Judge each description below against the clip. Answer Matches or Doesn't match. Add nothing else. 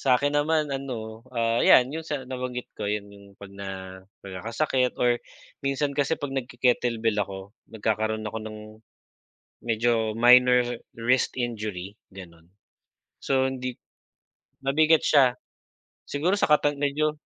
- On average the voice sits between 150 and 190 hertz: Doesn't match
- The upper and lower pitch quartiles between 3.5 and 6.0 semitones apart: Matches